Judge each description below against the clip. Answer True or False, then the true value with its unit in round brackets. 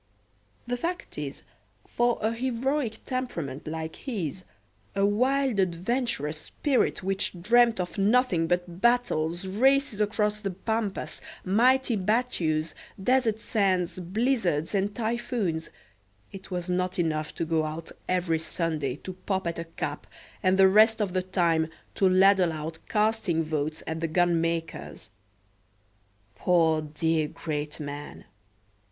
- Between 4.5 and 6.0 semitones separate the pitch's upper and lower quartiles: True (5.4 semitones)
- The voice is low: False (185 Hz)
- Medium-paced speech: False (130 wpm)